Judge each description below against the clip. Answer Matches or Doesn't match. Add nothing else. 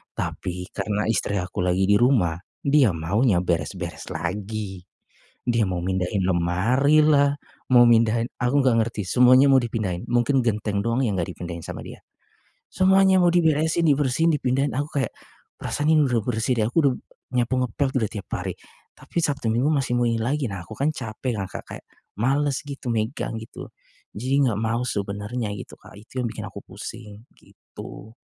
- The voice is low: Matches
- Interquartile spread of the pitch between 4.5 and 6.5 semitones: Matches